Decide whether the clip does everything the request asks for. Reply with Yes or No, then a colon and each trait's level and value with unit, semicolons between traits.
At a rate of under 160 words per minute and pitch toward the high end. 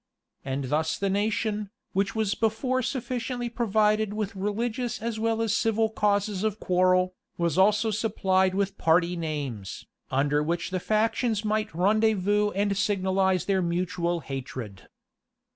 Yes: slow, 135 wpm; high, 200 Hz